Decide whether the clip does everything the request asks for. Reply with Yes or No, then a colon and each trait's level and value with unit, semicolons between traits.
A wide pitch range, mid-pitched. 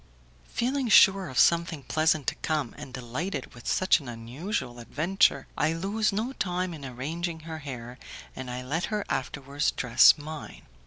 Yes: wide, 5.8 semitones; medium, 155 Hz